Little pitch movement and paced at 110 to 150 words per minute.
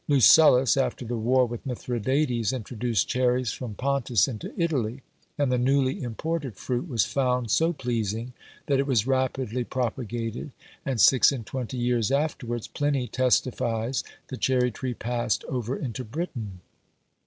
Yes: narrow, 2.3 semitones; average, 140 wpm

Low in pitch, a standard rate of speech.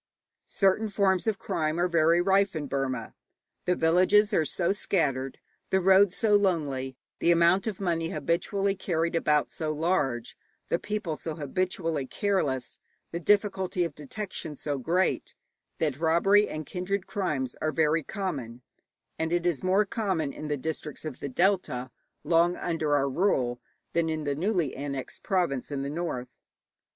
No: medium, 165 Hz; average, 155 wpm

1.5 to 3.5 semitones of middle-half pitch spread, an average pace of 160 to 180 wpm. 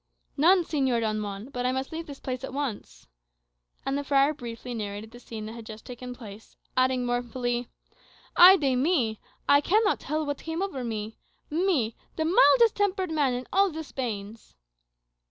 No: average, 5.3 semitones; average, 175 wpm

